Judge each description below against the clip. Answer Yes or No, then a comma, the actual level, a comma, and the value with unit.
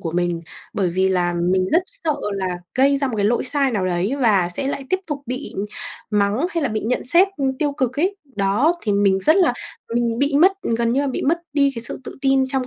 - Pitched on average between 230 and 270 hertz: Yes, very high, 250 Hz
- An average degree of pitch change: No, wide, 6.4 semitones